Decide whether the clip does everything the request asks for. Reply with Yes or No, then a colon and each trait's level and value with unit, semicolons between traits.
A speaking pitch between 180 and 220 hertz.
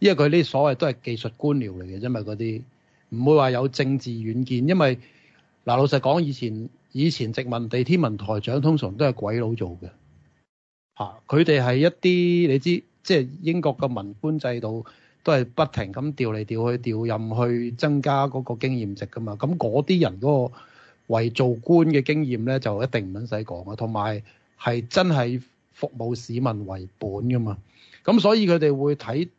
No: low, 125 Hz